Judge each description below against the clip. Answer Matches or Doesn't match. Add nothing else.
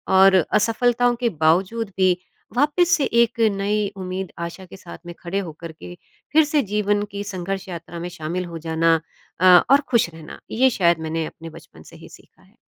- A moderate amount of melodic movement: Matches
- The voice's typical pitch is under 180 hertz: Doesn't match